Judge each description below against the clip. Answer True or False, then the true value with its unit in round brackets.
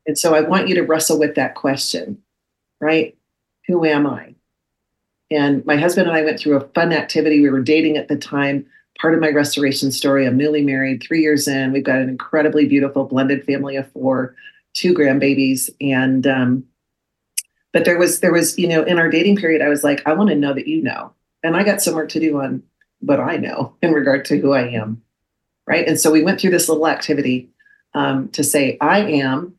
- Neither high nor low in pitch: True (150 Hz)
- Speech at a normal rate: False (215 wpm)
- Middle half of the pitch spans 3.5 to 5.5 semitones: False (2.9 semitones)